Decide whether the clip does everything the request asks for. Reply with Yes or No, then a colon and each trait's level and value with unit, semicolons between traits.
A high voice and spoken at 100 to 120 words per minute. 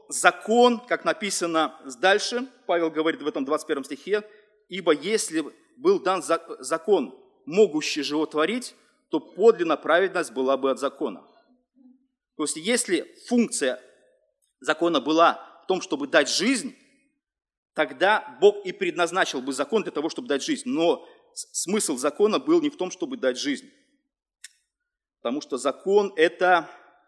No: high, 210 Hz; average, 135 wpm